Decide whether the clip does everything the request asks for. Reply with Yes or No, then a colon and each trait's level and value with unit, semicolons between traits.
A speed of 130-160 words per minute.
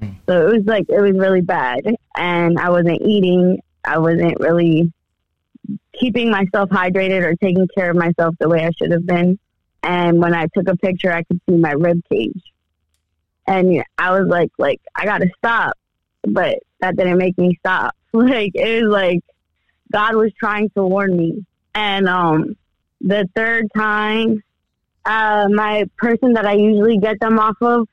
No: average, 170 wpm